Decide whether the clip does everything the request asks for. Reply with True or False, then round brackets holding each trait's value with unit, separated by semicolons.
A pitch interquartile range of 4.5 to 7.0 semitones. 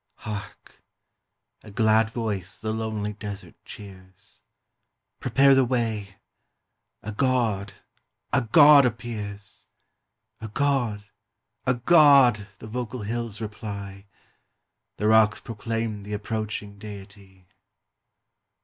False (2.6 semitones)